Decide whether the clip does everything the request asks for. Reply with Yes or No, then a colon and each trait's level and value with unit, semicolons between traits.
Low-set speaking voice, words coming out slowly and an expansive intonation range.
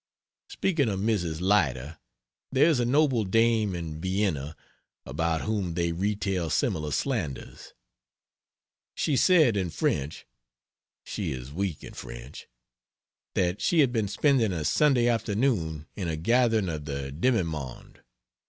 Yes: very low, 95 Hz; slow, 130 wpm; wide, 6.8 semitones